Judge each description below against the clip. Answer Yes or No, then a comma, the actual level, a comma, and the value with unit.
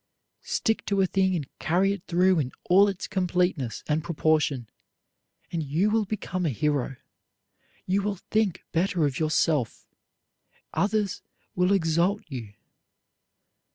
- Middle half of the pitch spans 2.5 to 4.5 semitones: Yes, average, 4.2 semitones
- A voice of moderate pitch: Yes, medium, 175 Hz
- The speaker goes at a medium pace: No, slow, 130 wpm